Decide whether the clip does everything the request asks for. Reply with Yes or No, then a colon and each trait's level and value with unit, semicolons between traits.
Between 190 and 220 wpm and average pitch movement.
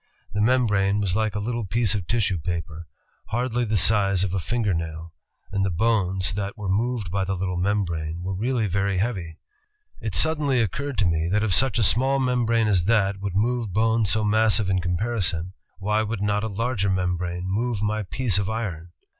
Yes: average, 195 wpm; average, 3.6 semitones